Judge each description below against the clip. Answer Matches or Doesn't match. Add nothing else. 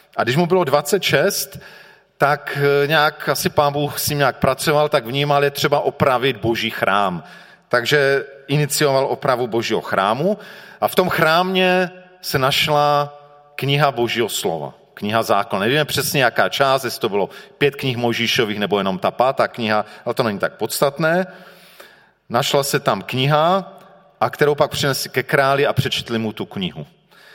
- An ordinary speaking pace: Matches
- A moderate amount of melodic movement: Matches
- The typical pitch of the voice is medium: Matches